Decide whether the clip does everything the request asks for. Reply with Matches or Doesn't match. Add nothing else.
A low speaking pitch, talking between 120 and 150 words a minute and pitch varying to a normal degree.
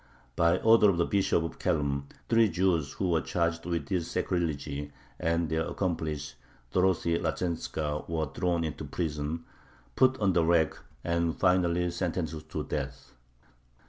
Doesn't match